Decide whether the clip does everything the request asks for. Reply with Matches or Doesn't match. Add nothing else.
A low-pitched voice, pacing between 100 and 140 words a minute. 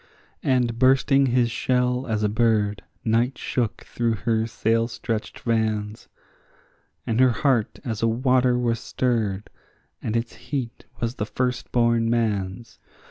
Matches